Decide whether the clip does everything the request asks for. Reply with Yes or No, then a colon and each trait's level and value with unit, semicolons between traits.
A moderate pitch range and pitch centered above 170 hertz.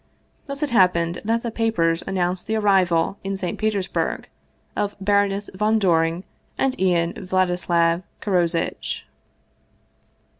Yes: average, 3.2 semitones; high, 190 Hz